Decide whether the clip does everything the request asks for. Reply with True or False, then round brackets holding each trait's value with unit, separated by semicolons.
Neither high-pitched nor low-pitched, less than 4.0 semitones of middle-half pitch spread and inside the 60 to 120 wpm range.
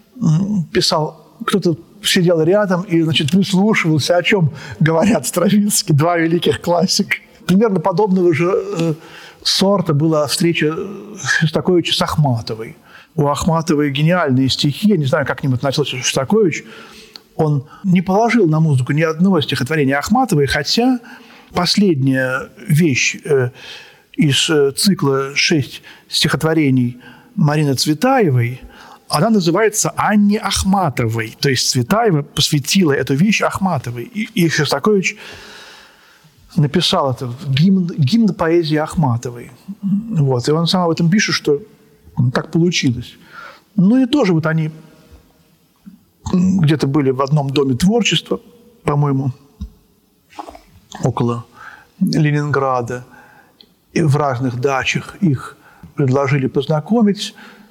False (165 Hz; 5.5 semitones; 110 wpm)